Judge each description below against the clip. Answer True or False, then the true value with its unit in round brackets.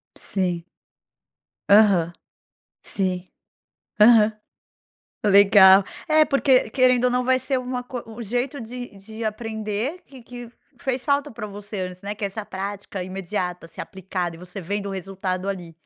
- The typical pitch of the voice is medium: False (210 Hz)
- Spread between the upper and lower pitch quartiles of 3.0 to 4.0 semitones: False (4.4 semitones)